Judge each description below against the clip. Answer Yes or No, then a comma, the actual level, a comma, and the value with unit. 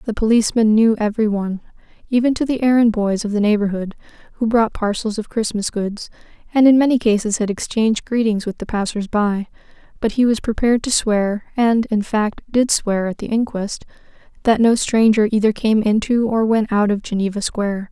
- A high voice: Yes, high, 220 Hz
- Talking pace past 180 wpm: Yes, average, 190 wpm